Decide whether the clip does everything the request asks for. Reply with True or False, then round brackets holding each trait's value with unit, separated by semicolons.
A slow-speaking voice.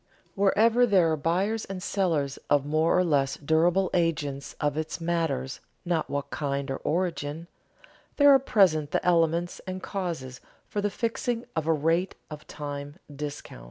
False (160 wpm)